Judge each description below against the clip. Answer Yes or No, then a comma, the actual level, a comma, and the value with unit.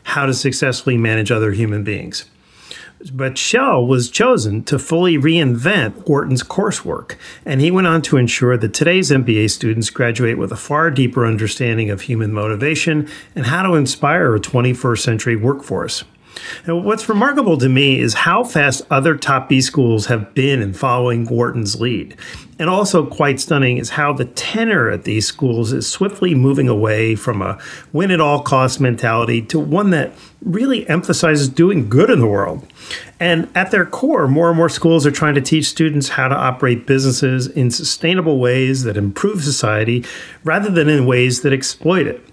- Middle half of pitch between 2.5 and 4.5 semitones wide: No, average, 4.9 semitones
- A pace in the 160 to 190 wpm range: Yes, average, 175 wpm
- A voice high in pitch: No, low, 135 Hz